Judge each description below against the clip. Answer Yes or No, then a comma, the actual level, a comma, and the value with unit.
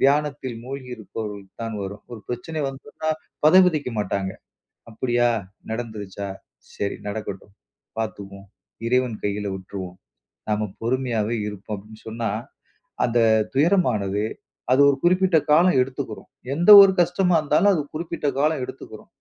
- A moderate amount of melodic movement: No, wide, 6.3 semitones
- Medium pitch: No, low, 120 Hz